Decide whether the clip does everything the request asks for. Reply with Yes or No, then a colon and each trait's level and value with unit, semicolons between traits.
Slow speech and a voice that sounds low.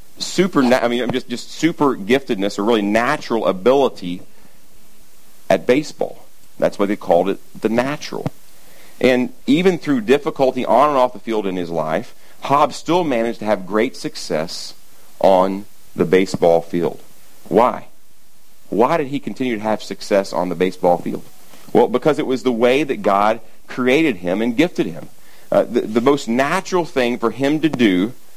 No: average, 165 wpm; low, 115 Hz